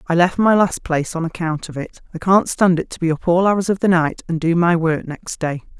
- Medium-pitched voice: Yes, medium, 170 Hz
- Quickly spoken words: Yes, fast, 280 wpm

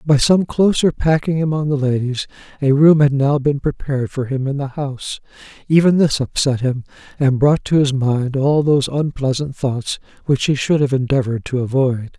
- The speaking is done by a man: Yes, male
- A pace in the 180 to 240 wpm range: Yes, average, 185 wpm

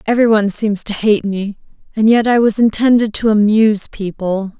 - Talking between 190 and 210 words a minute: No, average, 170 wpm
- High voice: Yes, high, 215 Hz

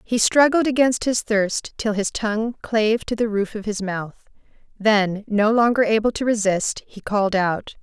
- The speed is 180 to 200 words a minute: Yes, average, 185 wpm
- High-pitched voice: Yes, high, 215 Hz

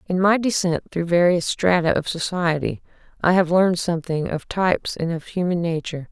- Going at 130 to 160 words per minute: No, average, 175 wpm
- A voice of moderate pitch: Yes, medium, 175 Hz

